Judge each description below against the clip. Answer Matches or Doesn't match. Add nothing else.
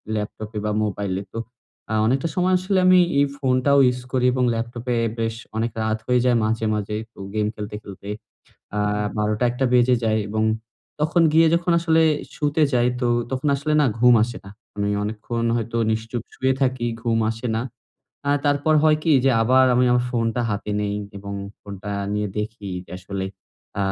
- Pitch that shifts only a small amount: Doesn't match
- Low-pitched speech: Matches